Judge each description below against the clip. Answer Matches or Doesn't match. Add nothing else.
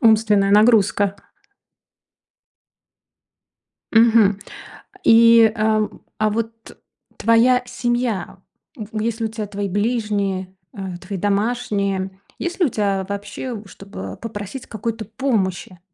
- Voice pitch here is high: Matches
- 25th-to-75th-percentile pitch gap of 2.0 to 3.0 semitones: Matches